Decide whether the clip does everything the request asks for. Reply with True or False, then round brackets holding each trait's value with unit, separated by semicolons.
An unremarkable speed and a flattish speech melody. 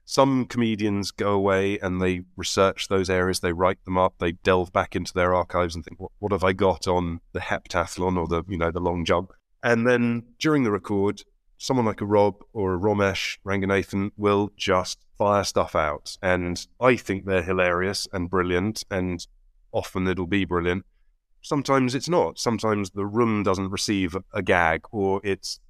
True (180 wpm; 2.1 semitones)